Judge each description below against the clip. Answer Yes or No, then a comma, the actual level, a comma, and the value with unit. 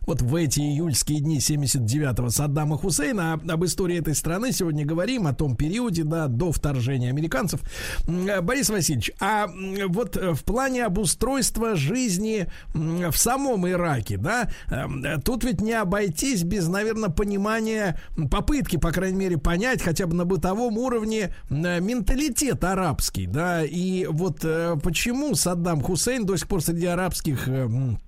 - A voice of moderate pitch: Yes, medium, 175 Hz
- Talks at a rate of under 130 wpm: No, average, 135 wpm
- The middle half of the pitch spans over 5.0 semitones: Yes, wide, 5.4 semitones